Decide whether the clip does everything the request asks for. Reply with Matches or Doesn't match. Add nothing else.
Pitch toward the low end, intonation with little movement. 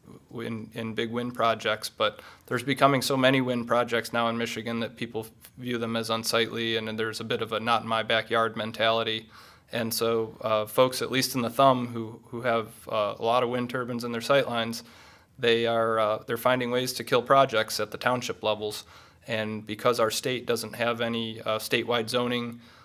Matches